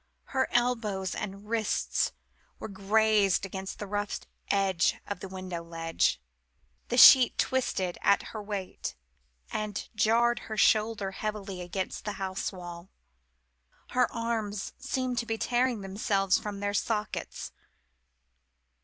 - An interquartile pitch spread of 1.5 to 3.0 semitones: Yes, average, 2.7 semitones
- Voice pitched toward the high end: Yes, high, 205 Hz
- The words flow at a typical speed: No, slow, 125 wpm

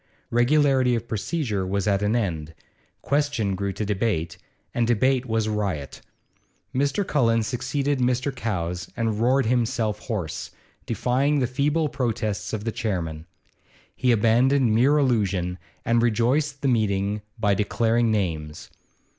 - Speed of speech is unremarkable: No, slow, 130 wpm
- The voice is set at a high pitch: No, low, 115 Hz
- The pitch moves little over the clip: No, average, 4.4 semitones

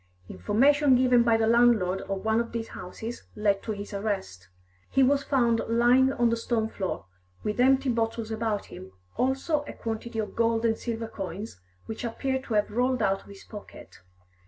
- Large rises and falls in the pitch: No, average, 2.8 semitones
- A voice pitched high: Yes, high, 230 Hz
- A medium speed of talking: Yes, average, 180 wpm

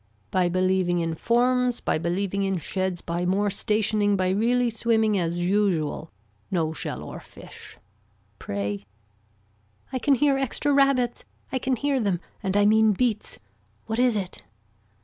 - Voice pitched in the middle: No, high, 205 Hz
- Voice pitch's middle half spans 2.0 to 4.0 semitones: No, average, 5.2 semitones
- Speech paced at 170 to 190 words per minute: No, average, 150 wpm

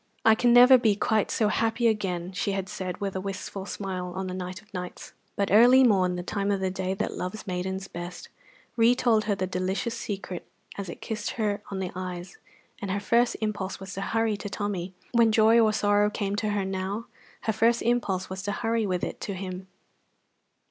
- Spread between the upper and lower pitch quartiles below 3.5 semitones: Yes, average, 2.7 semitones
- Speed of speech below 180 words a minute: No, fast, 205 wpm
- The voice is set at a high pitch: Yes, high, 200 Hz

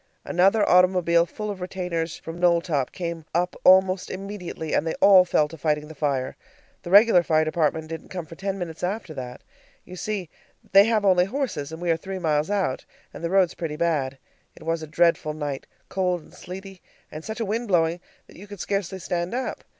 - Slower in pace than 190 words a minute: No, average, 200 wpm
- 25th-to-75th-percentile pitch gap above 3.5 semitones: No, average, 3.1 semitones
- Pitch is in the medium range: Yes, medium, 175 Hz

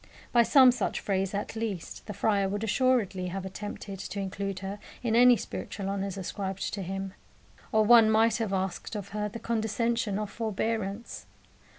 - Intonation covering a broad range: No, narrow, 2.6 semitones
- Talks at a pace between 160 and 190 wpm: Yes, average, 170 wpm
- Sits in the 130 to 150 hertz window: No, high, 205 Hz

